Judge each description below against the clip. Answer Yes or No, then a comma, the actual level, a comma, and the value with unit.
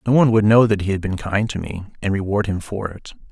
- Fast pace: Yes, fast, 290 wpm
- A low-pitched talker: Yes, low, 100 Hz